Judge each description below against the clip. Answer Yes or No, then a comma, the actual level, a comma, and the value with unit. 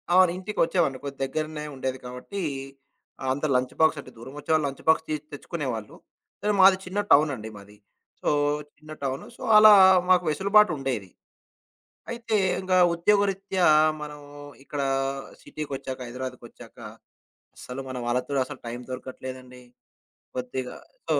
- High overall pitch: No, medium, 145 Hz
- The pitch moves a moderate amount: No, wide, 5.8 semitones